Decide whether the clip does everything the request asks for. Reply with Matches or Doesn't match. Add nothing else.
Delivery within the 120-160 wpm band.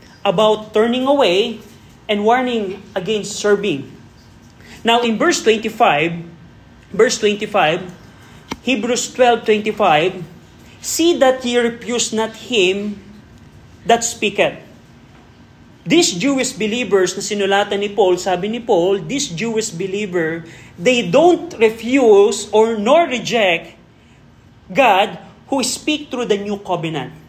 Doesn't match